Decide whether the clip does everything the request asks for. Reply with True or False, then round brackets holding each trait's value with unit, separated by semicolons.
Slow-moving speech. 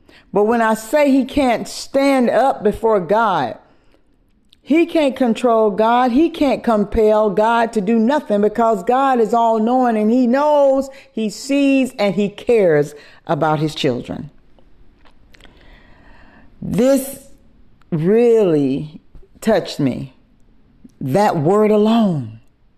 True (115 wpm)